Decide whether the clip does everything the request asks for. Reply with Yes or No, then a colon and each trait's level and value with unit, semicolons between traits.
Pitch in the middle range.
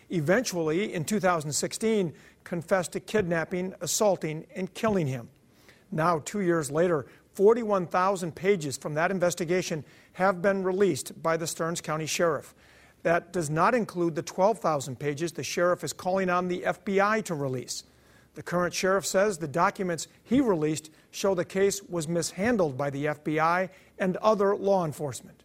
Yes: medium, 175 Hz